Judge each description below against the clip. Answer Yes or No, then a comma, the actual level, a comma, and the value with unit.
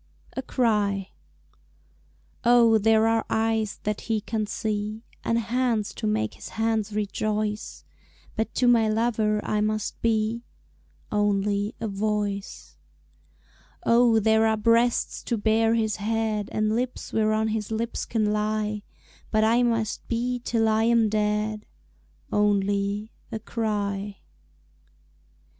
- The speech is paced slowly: Yes, slow, 125 wpm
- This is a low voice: No, high, 215 Hz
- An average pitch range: No, narrow, 1.4 semitones